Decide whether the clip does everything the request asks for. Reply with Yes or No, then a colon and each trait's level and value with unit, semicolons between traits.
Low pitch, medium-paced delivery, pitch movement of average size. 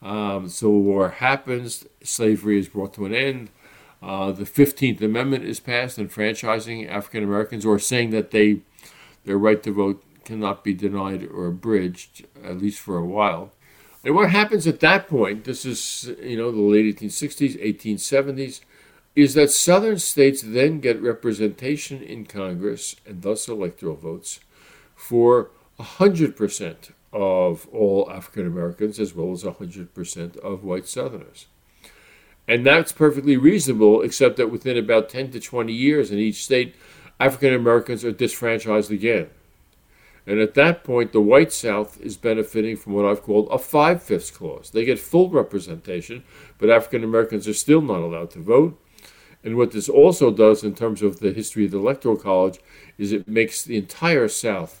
Yes: low, 110 Hz; average, 160 wpm; average, 4.2 semitones